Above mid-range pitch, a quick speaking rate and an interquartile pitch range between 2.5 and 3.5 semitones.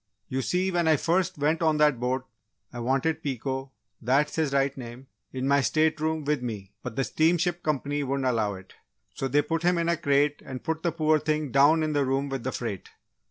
No: medium, 145 Hz; fast, 215 wpm; average, 3.2 semitones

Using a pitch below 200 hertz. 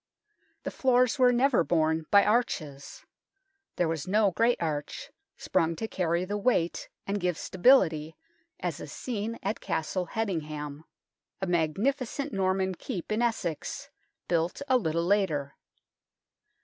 Yes: medium, 185 Hz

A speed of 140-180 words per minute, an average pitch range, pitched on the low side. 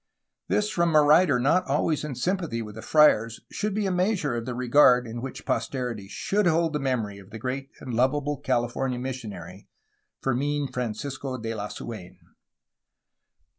Yes: average, 165 wpm; average, 4.5 semitones; low, 130 Hz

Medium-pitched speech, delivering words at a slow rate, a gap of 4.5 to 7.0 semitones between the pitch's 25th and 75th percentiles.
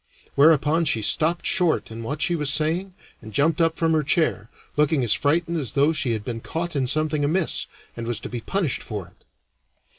No: medium, 150 Hz; fast, 205 wpm; average, 5.1 semitones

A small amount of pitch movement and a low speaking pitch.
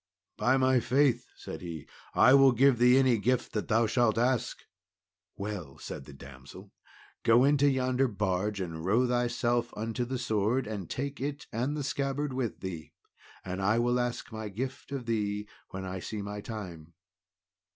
No: average, 4.2 semitones; low, 115 Hz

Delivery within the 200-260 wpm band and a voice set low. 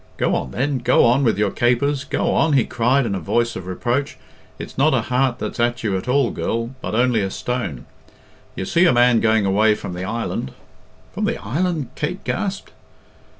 Yes: fast, 205 wpm; low, 120 Hz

